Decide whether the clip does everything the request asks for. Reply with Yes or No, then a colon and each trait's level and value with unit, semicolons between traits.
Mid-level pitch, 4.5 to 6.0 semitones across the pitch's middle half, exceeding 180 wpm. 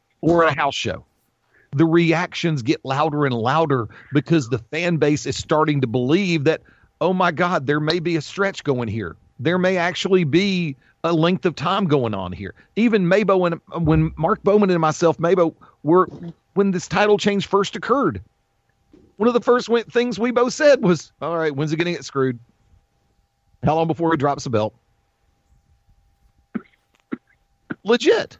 No: medium, 165 Hz; wide, 5.4 semitones; average, 170 wpm